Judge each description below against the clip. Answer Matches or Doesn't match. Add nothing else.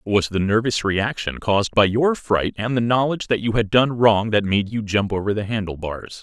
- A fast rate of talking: Matches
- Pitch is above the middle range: Doesn't match